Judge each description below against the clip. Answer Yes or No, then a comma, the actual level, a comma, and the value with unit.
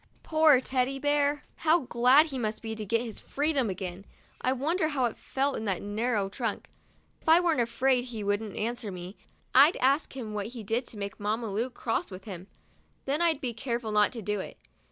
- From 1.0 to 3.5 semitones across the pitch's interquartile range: No, average, 4.5 semitones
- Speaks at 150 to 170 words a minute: No, fast, 205 wpm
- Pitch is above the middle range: Yes, high, 240 Hz